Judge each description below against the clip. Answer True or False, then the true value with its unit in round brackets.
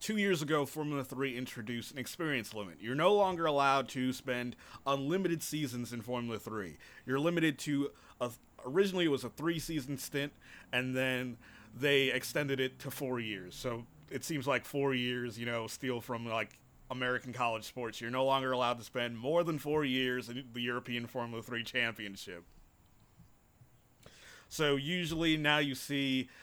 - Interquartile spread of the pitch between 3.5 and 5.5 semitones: False (3.0 semitones)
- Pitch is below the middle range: True (130 Hz)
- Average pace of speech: True (170 wpm)